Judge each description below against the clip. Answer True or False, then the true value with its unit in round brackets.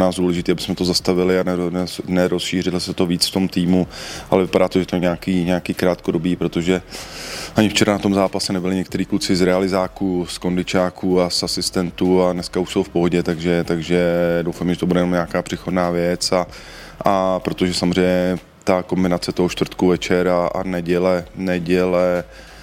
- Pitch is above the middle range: False (90 Hz)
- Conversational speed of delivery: False (175 wpm)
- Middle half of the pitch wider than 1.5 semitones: False (0.8 semitones)